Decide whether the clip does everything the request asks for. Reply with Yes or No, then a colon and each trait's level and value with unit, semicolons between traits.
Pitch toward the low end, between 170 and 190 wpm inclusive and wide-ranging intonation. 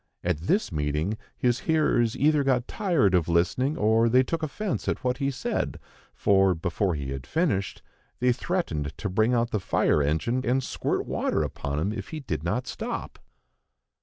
Yes: low, 115 Hz; average, 175 wpm; wide, 7.6 semitones